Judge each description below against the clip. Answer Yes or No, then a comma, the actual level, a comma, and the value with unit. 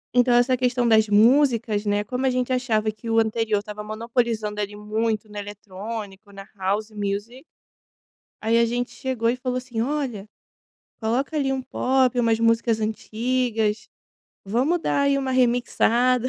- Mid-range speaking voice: No, high, 230 Hz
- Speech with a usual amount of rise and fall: Yes, average, 3.0 semitones